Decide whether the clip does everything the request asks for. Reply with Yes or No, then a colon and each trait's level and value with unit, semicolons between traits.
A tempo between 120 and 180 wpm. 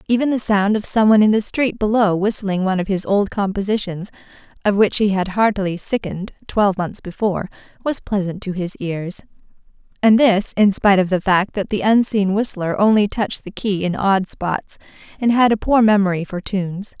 No: average, 190 wpm